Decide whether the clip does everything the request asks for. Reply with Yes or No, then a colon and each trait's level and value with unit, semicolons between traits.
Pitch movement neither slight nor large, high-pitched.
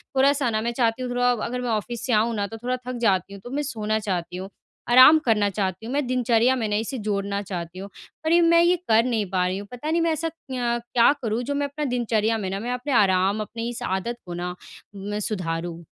Yes: average, 3.9 semitones; high, 225 Hz